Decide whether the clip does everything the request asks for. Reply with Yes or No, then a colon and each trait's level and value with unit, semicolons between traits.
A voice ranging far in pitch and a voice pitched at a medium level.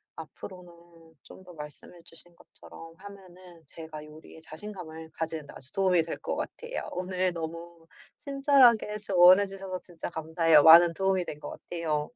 No: average, 2.7 semitones; medium, 170 Hz